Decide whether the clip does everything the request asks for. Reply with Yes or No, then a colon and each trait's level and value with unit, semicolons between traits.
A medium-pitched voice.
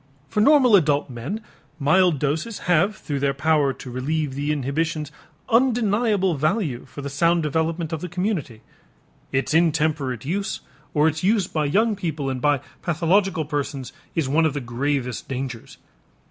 Yes: medium, 155 Hz